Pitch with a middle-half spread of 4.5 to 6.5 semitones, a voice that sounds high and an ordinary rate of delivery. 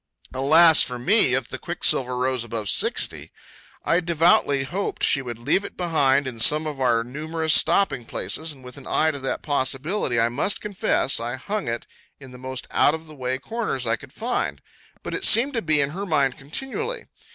No: average, 4.8 semitones; medium, 140 Hz; average, 195 wpm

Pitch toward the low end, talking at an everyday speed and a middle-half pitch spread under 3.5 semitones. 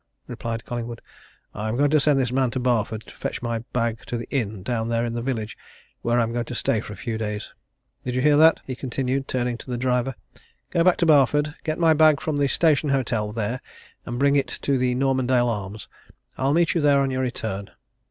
No: low, 125 Hz; fast, 220 wpm; average, 3.1 semitones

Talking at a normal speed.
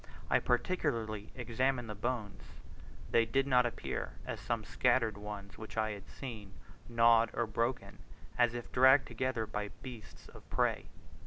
Yes: average, 150 wpm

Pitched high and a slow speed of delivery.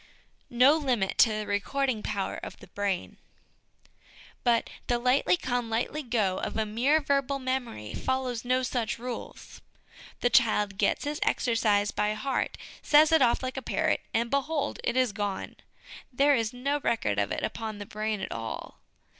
No: high, 240 Hz; average, 170 wpm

